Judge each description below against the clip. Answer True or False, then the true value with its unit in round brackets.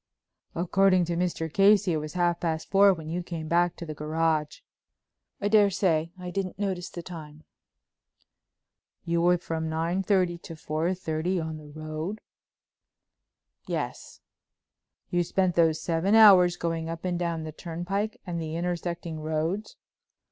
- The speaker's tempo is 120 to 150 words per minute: True (140 wpm)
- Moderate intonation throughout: False (2.3 semitones)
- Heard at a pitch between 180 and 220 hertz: False (170 Hz)